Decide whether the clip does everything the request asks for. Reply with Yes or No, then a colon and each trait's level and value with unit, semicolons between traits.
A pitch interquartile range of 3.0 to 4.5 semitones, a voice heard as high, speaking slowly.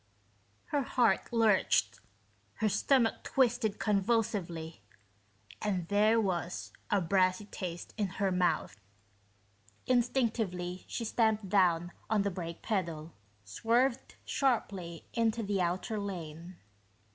Yes: average, 4.1 semitones; high, 200 Hz; slow, 105 wpm